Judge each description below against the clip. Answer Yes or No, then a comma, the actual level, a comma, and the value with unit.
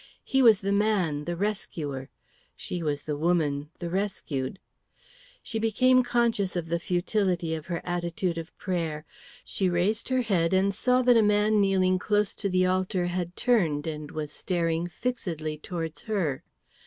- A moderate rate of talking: Yes, average, 160 wpm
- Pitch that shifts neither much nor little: Yes, average, 4.2 semitones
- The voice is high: No, medium, 180 Hz